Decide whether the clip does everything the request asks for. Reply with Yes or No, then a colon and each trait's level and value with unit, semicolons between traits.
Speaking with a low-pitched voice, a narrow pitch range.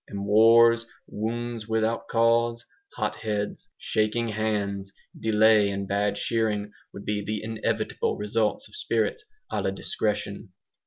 Yes: low, 110 Hz; narrow, 2.0 semitones